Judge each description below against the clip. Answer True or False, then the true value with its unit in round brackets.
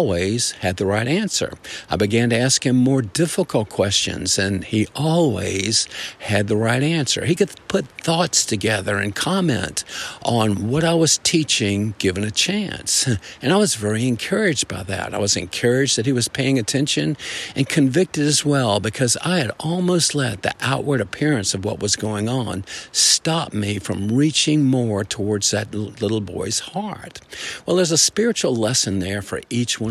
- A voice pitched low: True (120 Hz)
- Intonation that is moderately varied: False (6.4 semitones)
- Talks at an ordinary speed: True (175 wpm)